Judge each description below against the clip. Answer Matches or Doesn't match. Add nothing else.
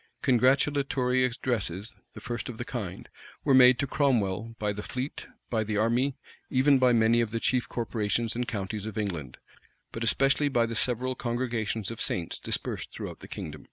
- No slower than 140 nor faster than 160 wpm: Doesn't match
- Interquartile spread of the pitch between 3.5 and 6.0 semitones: Doesn't match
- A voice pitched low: Matches